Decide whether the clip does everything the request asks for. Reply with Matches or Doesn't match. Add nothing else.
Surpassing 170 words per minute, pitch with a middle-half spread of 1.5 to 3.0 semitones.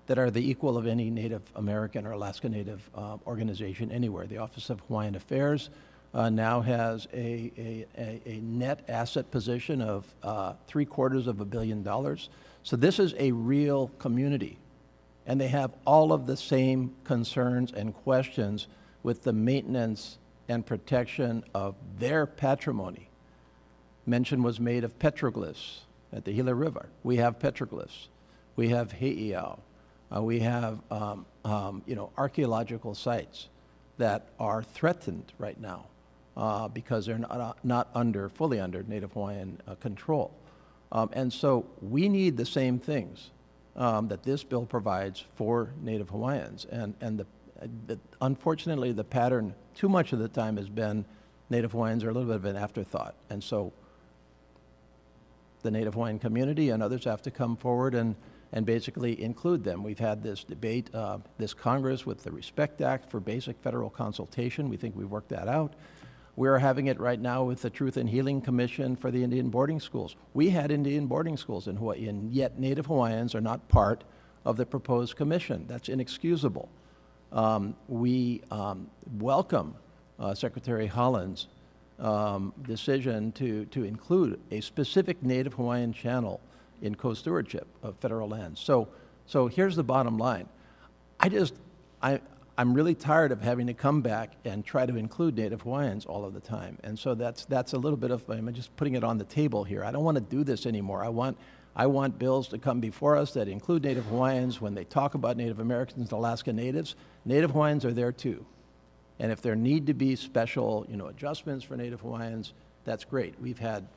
Doesn't match